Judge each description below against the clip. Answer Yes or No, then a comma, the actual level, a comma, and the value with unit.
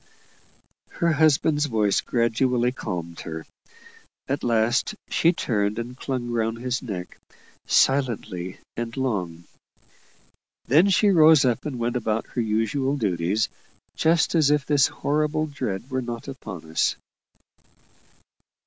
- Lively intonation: No, average, 4.7 semitones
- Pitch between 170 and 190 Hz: No, low, 120 Hz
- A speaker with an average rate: No, slow, 120 wpm